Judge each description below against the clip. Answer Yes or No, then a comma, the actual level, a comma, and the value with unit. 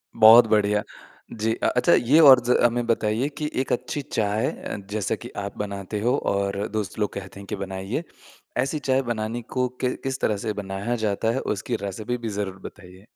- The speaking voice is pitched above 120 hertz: No, low, 110 Hz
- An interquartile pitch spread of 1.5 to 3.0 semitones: No, average, 3.5 semitones